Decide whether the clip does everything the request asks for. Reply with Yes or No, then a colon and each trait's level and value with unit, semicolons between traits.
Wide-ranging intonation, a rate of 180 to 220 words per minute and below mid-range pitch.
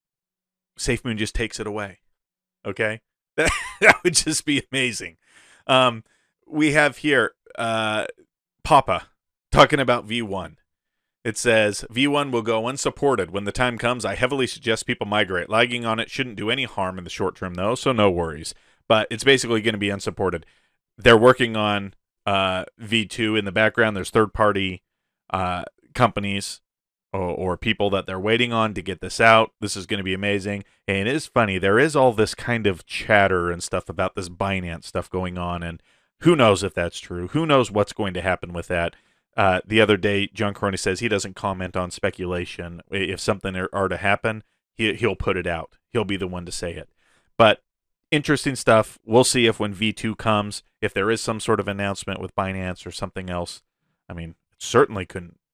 No: average, 3.9 semitones; average, 190 wpm; low, 105 Hz